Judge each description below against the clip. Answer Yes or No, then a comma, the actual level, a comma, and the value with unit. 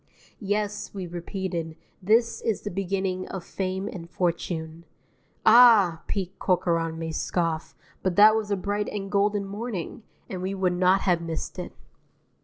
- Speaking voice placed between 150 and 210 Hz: Yes, high, 190 Hz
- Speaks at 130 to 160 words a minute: Yes, average, 150 wpm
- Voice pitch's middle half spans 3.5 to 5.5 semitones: No, average, 2.9 semitones